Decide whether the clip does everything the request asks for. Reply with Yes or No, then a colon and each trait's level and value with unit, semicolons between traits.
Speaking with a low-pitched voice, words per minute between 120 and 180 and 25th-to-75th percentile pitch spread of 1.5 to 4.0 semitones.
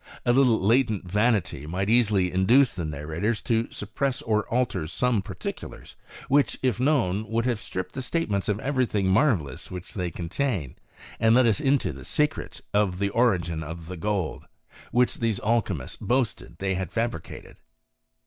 No: low, 105 Hz; average, 170 wpm; average, 5.1 semitones